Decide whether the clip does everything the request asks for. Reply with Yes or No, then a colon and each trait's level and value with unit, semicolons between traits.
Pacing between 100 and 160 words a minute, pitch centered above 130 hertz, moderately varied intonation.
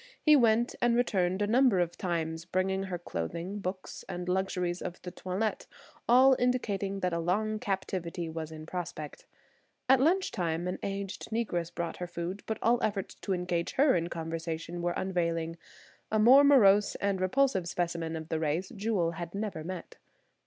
No: average, 170 wpm; medium, 185 Hz; average, 3.9 semitones